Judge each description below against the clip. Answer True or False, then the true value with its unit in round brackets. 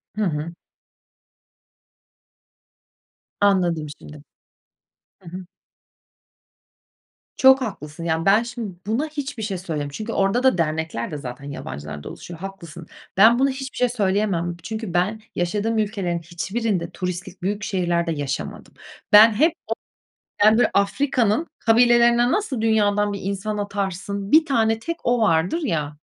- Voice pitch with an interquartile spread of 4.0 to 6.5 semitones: True (5.0 semitones)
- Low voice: False (200 Hz)